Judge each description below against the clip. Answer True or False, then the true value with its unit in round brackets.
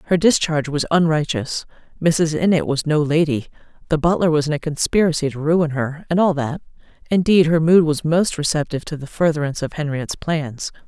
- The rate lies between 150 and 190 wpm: True (175 wpm)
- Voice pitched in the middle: True (155 Hz)